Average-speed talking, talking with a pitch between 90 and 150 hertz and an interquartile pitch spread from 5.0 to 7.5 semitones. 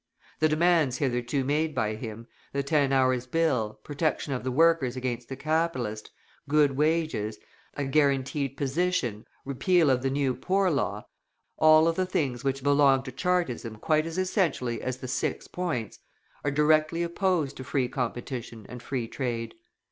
No: average, 155 wpm; medium, 140 Hz; average, 4.0 semitones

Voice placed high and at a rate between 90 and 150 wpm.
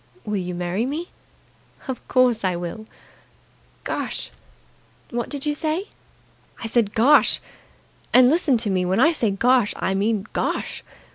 Yes: high, 230 Hz; average, 145 wpm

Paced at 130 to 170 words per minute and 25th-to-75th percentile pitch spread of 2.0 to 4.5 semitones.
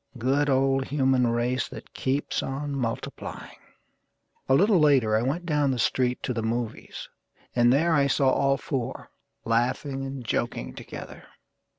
Yes: average, 150 wpm; narrow, 2.4 semitones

